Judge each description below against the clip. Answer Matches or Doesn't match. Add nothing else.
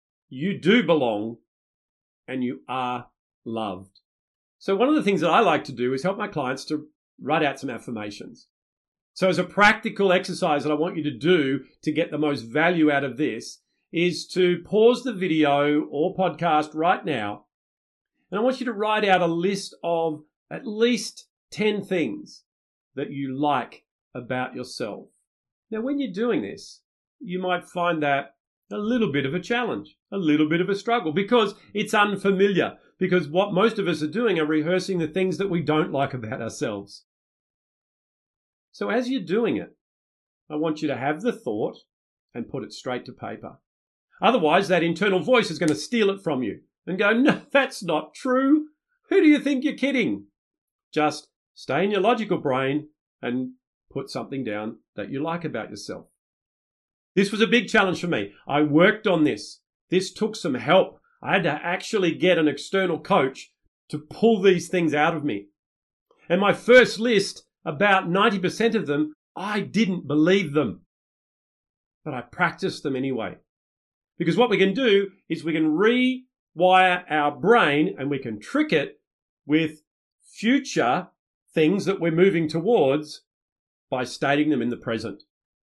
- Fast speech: Doesn't match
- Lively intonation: Matches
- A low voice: Doesn't match